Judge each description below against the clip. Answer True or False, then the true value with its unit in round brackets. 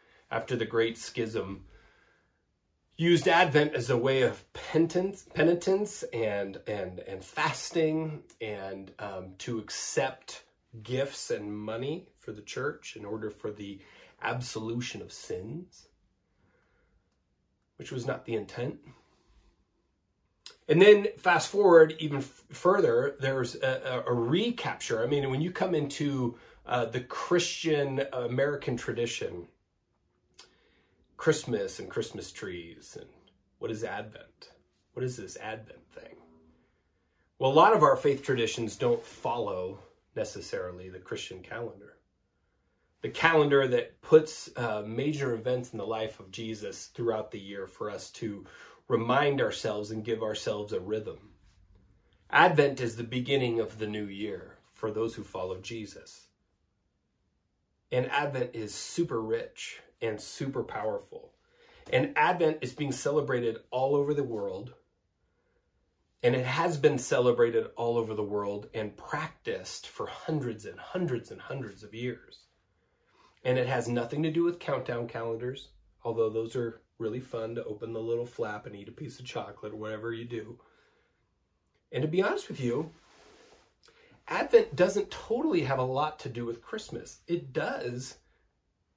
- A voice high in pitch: False (125 Hz)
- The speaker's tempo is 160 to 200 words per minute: False (140 wpm)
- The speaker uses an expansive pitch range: True (6.8 semitones)